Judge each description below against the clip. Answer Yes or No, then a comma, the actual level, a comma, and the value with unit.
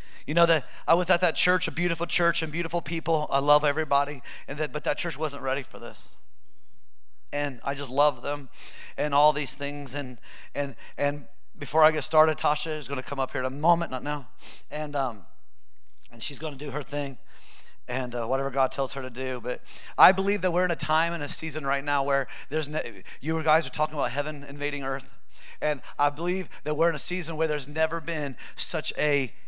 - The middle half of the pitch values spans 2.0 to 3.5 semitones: Yes, average, 2.8 semitones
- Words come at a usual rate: No, fast, 220 wpm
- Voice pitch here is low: No, medium, 145 Hz